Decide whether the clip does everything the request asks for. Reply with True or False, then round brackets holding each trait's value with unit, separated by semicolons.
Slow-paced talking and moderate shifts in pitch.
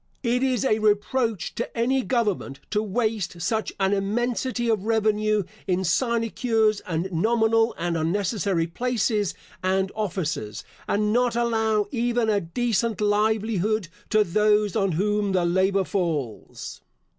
True (130 wpm; 3.2 semitones)